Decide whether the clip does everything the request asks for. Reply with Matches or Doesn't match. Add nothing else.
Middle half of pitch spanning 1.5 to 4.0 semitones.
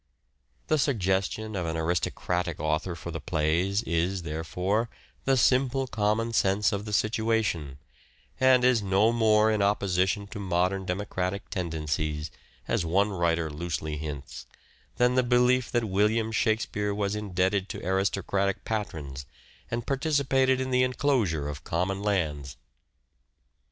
Doesn't match